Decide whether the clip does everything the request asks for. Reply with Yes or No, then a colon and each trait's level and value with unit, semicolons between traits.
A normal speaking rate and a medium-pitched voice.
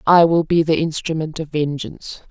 Yes: average, 180 wpm; medium, 160 Hz